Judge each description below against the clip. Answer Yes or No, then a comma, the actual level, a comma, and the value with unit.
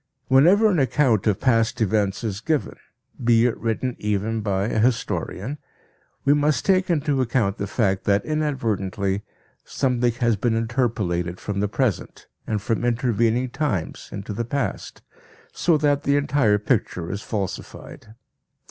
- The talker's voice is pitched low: Yes, low, 115 Hz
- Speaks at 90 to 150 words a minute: Yes, average, 145 wpm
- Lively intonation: No, average, 4.7 semitones